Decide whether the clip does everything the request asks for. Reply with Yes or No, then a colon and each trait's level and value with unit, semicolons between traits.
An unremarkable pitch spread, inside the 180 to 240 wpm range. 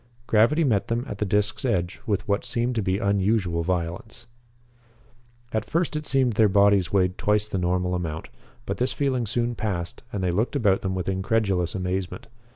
Yes: average, 3.8 semitones; average, 185 wpm